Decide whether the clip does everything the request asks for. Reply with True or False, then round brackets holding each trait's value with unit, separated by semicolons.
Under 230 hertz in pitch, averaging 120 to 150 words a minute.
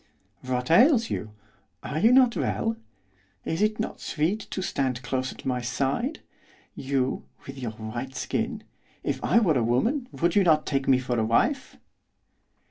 False (140 Hz; 165 wpm)